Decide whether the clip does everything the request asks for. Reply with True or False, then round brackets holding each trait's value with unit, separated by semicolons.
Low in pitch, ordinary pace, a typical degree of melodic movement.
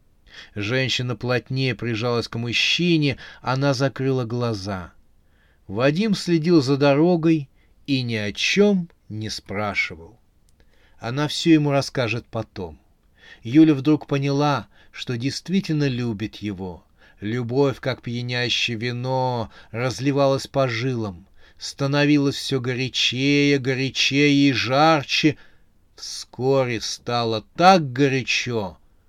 False (125 Hz; 95 wpm; 4.6 semitones)